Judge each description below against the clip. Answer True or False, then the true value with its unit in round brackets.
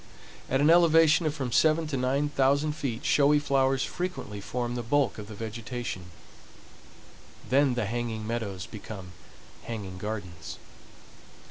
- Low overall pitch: True (125 Hz)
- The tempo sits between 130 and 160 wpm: True (135 wpm)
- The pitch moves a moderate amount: True (4.9 semitones)